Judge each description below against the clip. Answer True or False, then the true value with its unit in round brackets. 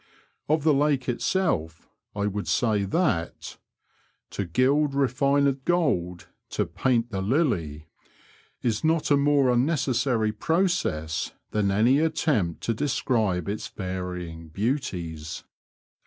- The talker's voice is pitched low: True (120 Hz)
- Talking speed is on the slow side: True (120 wpm)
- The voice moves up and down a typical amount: False (7.4 semitones)